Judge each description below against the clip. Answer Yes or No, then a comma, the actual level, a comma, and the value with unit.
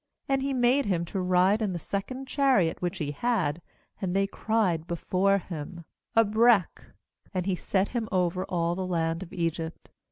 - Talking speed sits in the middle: Yes, average, 170 wpm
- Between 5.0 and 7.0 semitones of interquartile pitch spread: No, average, 4.4 semitones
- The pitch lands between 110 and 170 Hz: No, medium, 185 Hz